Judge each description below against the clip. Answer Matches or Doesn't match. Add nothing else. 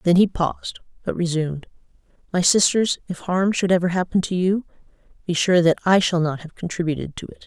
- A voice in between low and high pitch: Matches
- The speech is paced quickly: Doesn't match